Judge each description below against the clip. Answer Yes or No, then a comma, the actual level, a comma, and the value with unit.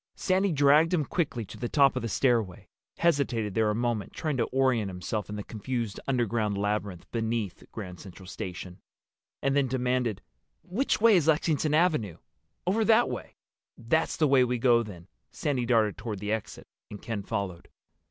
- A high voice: No, low, 120 Hz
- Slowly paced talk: No, average, 170 wpm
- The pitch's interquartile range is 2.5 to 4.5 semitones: No, average, 5.3 semitones